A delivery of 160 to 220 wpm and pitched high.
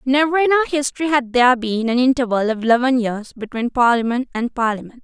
Yes: average, 190 wpm; very high, 250 Hz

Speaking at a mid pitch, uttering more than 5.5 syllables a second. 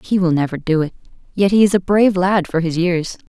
Yes: medium, 180 Hz; 5.9 syllables/s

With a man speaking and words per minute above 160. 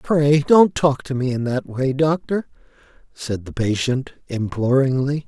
No: male; average, 150 wpm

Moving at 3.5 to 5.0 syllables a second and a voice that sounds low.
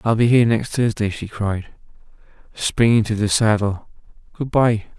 Yes: 4.7 syllables/s; low, 110 Hz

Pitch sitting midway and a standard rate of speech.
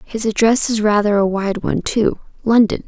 No: high, 215 Hz; average, 165 wpm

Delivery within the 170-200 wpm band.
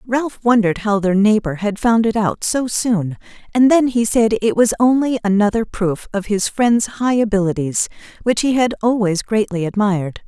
Yes: average, 180 wpm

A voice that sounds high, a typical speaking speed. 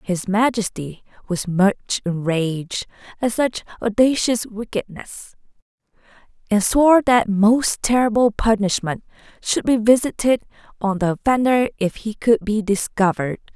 No: high, 215 Hz; slow, 115 wpm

